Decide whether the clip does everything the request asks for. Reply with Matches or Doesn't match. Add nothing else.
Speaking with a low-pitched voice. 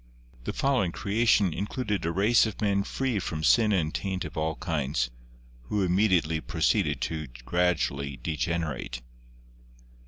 Matches